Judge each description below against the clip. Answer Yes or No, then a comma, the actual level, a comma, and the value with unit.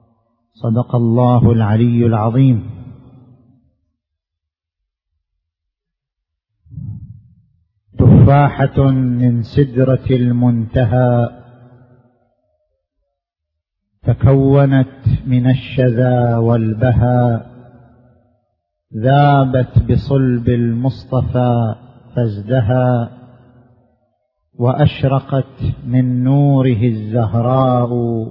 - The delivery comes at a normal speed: No, slow, 40 wpm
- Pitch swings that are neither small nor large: No, narrow, 1.9 semitones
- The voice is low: Yes, low, 120 Hz